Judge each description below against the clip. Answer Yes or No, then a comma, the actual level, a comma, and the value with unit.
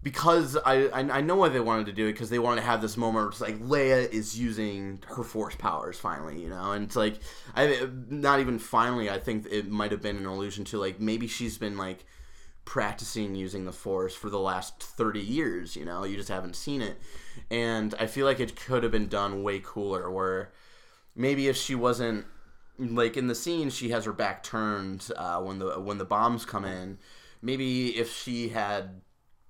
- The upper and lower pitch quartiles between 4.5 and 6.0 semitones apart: No, average, 3.6 semitones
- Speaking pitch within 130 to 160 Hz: No, low, 110 Hz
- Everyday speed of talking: No, fast, 210 wpm